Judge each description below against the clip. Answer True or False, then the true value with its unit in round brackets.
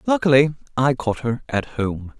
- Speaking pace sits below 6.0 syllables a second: True (4.5 syllables/s)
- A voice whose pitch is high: False (135 Hz)